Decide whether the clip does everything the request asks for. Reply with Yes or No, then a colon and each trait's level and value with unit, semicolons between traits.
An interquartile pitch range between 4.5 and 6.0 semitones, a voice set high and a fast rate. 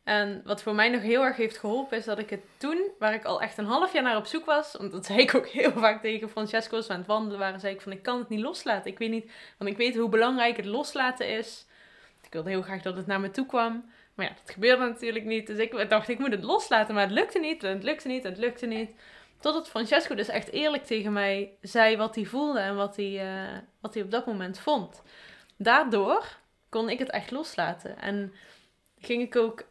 No: average, 3.6 semitones; high, 225 Hz; fast, 245 wpm